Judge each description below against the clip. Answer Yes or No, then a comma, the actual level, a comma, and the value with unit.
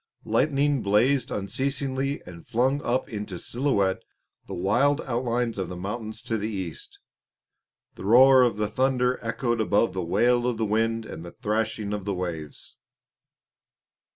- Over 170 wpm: No, average, 150 wpm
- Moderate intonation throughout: Yes, average, 4.1 semitones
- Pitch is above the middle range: No, low, 115 Hz